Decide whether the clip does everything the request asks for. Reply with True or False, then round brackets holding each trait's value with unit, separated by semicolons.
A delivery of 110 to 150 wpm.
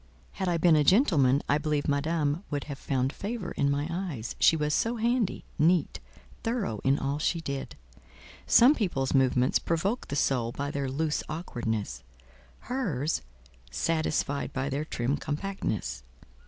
True (145 wpm)